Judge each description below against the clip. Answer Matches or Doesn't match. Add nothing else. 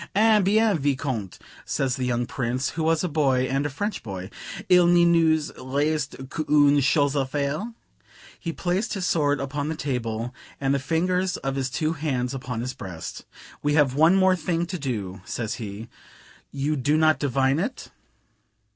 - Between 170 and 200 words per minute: Matches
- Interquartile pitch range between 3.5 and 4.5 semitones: Matches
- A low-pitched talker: Doesn't match